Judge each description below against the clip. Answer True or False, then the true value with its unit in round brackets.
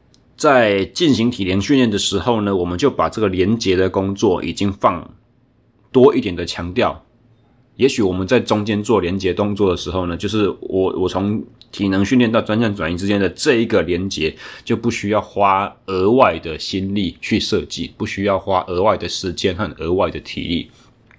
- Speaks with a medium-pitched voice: False (100 Hz)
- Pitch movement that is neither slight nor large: False (2.3 semitones)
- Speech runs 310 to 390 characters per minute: False (275 characters per minute)